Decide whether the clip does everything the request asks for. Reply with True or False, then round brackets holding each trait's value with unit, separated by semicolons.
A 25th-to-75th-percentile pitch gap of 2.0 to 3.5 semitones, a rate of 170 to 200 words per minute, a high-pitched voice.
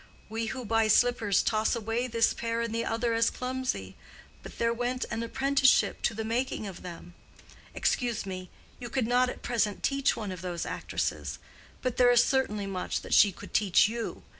True (2.7 semitones; 190 wpm; 230 Hz)